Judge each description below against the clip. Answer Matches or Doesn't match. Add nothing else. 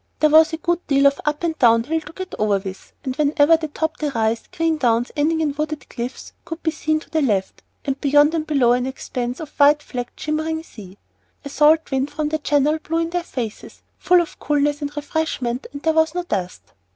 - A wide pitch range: Doesn't match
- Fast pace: Matches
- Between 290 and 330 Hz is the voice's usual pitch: Matches